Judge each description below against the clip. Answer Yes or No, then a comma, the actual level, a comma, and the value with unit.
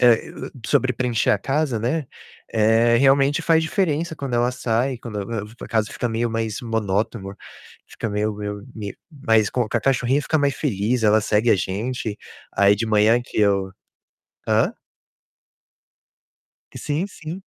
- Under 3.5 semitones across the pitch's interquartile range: No, average, 4.2 semitones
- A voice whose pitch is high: No, low, 115 Hz